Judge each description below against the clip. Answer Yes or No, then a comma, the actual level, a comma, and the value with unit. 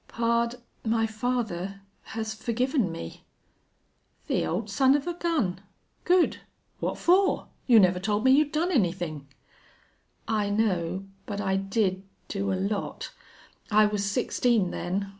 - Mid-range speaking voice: No, high, 215 Hz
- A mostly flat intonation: No, average, 4.3 semitones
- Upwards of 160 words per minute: No, slow, 135 wpm